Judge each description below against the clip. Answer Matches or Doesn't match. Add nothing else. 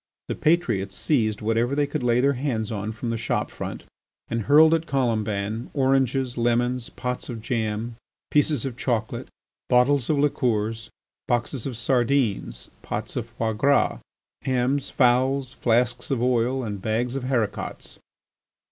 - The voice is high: Doesn't match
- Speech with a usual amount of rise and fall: Matches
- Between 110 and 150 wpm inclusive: Matches